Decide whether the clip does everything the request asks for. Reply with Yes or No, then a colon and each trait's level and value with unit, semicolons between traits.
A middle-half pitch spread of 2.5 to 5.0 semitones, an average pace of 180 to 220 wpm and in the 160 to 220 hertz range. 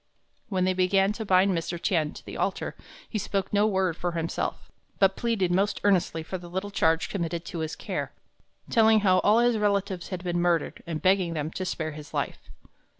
Yes: average, 2.9 semitones; average, 200 wpm; medium, 185 Hz